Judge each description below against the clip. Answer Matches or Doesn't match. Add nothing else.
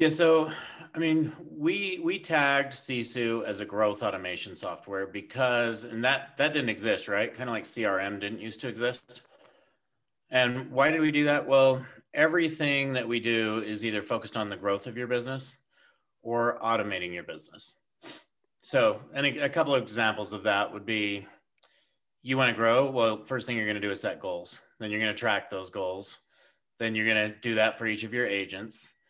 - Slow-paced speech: Doesn't match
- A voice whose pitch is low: Matches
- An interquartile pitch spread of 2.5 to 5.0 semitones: Matches